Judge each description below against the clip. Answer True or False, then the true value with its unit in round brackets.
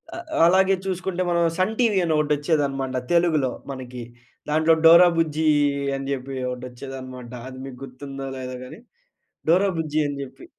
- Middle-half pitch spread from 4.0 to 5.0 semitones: True (4.6 semitones)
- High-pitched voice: False (145 Hz)